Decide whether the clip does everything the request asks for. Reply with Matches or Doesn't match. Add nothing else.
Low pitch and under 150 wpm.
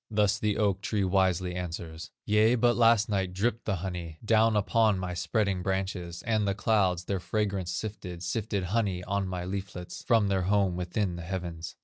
Doesn't match